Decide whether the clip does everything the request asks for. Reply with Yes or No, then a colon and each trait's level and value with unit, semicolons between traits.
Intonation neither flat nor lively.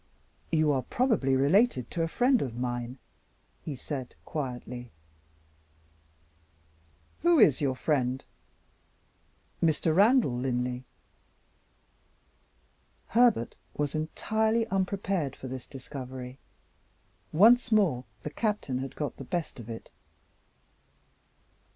No: wide, 7.7 semitones